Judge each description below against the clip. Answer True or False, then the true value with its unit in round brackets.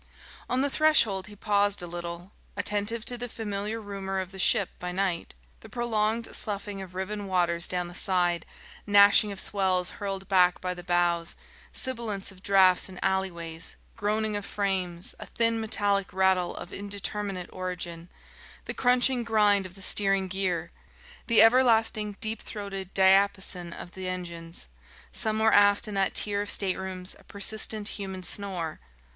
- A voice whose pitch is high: True (195 Hz)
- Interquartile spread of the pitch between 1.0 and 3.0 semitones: True (2.4 semitones)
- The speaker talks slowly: False (155 wpm)